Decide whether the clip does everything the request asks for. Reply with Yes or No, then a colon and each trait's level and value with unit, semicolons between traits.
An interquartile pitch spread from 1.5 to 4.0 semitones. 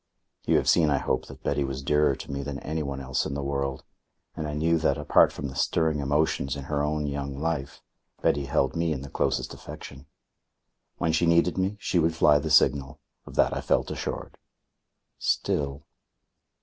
Yes: narrow, 2.4 semitones